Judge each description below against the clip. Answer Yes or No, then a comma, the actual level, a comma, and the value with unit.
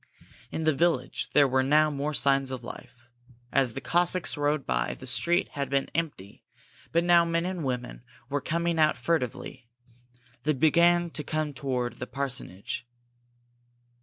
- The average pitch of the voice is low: No, medium, 145 Hz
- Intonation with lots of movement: No, average, 4.3 semitones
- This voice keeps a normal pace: Yes, average, 155 wpm